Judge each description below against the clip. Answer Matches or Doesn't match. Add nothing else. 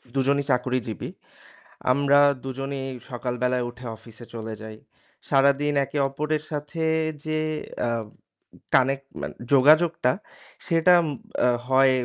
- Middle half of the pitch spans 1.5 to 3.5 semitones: Matches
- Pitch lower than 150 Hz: Matches